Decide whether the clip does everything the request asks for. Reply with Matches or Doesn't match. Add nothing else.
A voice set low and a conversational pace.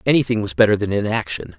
Matches